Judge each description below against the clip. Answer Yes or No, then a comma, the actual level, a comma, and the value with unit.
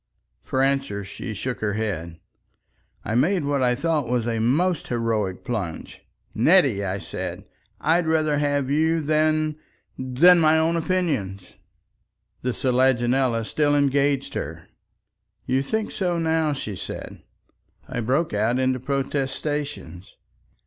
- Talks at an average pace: No, slow, 125 wpm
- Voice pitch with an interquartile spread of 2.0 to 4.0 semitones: No, average, 4.9 semitones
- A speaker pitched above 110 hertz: Yes, low, 135 Hz